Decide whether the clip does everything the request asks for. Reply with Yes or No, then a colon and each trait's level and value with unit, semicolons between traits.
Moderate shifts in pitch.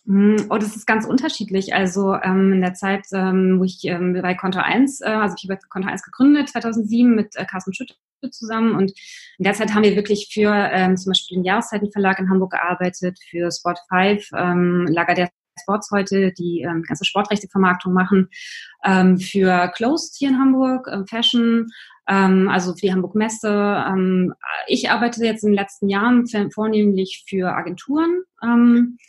Yes: average, 3.1 semitones